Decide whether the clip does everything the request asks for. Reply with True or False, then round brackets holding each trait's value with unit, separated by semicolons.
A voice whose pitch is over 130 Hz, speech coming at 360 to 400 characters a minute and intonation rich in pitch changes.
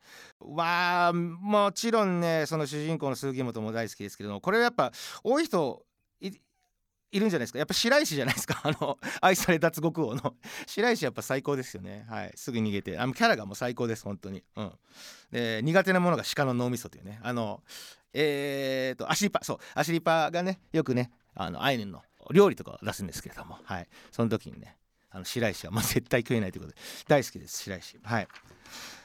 True (140 Hz; 395 characters per minute; 7.6 semitones)